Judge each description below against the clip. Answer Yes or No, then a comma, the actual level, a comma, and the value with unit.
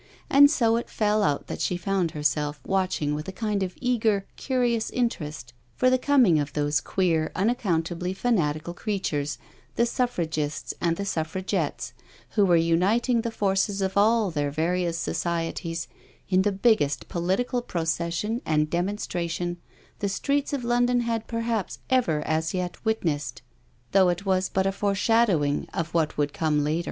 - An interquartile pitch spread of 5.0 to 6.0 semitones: Yes, wide, 5.6 semitones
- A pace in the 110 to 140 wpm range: No, average, 155 wpm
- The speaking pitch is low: No, medium, 185 Hz